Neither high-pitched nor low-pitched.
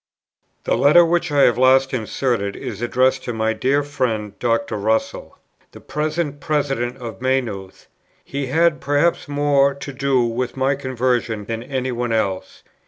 No: low, 130 Hz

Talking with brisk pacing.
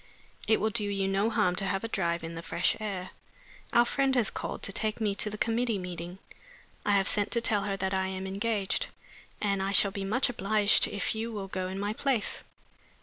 Yes: fast, 220 wpm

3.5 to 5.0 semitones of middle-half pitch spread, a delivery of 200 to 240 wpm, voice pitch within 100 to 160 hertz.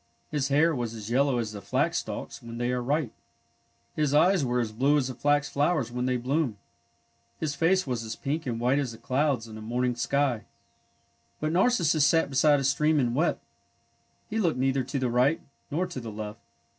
Yes: average, 3.8 semitones; fast, 205 wpm; low, 135 Hz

